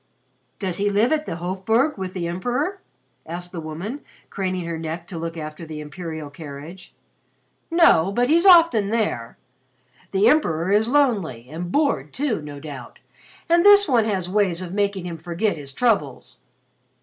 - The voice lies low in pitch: No, medium, 185 Hz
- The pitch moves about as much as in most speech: No, wide, 6.3 semitones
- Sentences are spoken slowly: No, average, 160 wpm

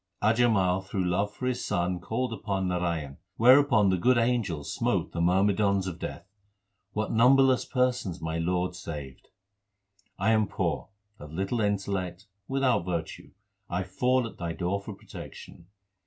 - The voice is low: Yes, very low, 95 Hz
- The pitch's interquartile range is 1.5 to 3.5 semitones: No, average, 4.5 semitones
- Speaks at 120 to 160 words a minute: Yes, average, 145 wpm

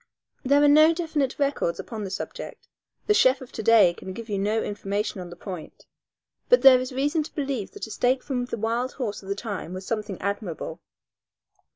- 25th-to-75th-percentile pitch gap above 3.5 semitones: Yes, average, 5.3 semitones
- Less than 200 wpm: No, fast, 205 wpm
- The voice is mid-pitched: No, high, 230 Hz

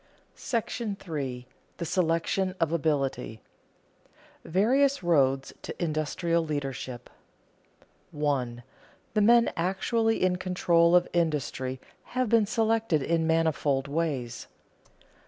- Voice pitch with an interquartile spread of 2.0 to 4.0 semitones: No, average, 5.3 semitones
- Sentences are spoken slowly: Yes, slow, 100 wpm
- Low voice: No, medium, 165 Hz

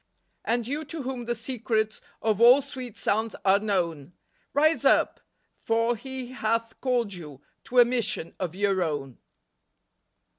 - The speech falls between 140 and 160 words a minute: Yes, average, 145 wpm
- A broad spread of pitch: No, average, 4.2 semitones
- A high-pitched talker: Yes, high, 225 Hz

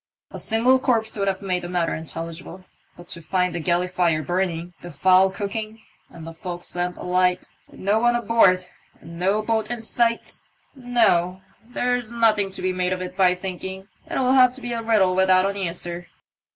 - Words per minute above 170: Yes, average, 190 wpm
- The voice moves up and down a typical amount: Yes, average, 3.9 semitones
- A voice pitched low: No, medium, 185 Hz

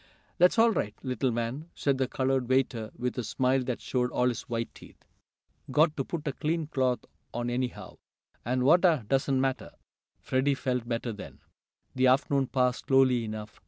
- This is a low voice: Yes, low, 130 Hz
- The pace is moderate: Yes, average, 170 wpm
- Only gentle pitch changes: Yes, narrow, 2.0 semitones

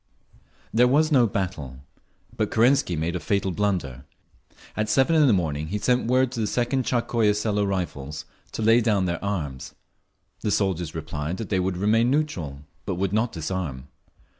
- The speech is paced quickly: No, average, 170 wpm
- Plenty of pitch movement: Yes, wide, 5.7 semitones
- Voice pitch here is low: Yes, low, 100 Hz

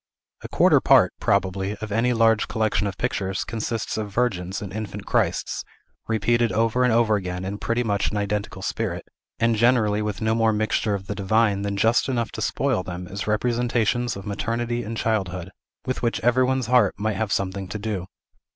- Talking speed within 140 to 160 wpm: No, average, 185 wpm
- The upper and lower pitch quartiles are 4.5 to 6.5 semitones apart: No, average, 2.8 semitones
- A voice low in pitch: Yes, low, 110 Hz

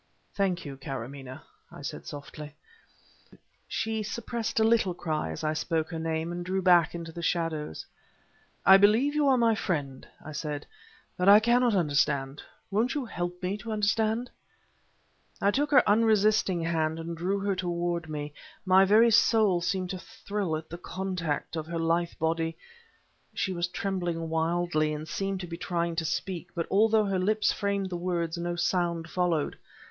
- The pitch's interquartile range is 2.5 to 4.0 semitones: Yes, average, 3.7 semitones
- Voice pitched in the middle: Yes, medium, 175 Hz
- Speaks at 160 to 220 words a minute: Yes, average, 170 wpm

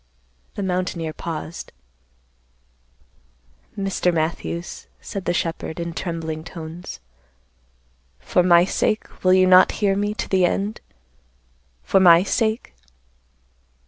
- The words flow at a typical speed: No, slow, 110 wpm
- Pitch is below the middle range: No, medium, 180 Hz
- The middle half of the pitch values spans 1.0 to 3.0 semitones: Yes, narrow, 2.6 semitones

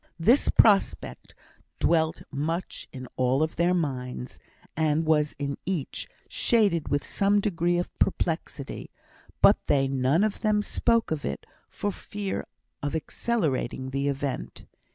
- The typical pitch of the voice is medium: Yes, medium, 160 Hz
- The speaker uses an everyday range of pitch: No, wide, 5.8 semitones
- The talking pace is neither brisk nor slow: No, slow, 130 wpm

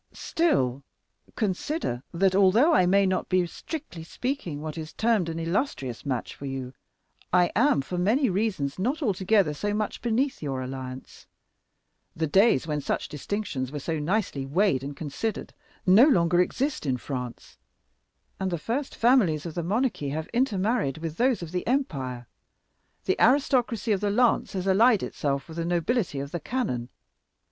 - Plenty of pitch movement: Yes, wide, 7.5 semitones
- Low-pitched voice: No, medium, 180 Hz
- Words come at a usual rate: Yes, average, 160 wpm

